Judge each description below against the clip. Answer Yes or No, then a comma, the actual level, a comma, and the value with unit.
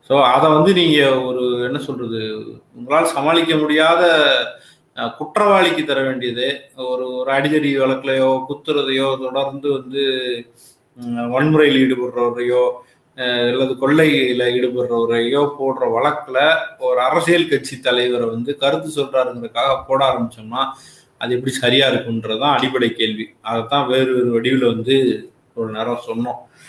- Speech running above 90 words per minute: Yes, average, 110 wpm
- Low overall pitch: Yes, low, 130 Hz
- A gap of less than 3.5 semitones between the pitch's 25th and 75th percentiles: Yes, narrow, 2.5 semitones